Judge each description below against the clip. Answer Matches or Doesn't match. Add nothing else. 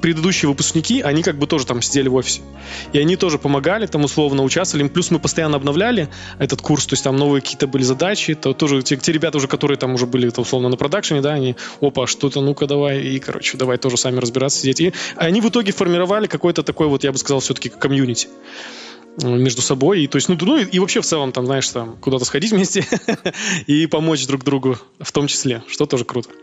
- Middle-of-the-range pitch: Matches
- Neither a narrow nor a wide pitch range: Matches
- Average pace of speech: Doesn't match